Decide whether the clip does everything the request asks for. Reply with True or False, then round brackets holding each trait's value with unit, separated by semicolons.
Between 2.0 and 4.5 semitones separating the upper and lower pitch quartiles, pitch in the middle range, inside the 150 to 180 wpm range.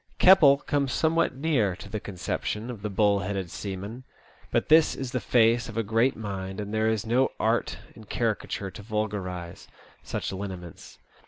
False (4.0 semitones; 110 Hz; 170 wpm)